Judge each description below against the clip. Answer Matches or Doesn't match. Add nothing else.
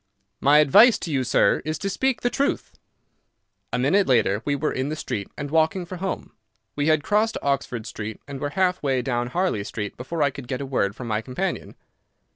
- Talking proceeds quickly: Matches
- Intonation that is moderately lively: Doesn't match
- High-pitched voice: Doesn't match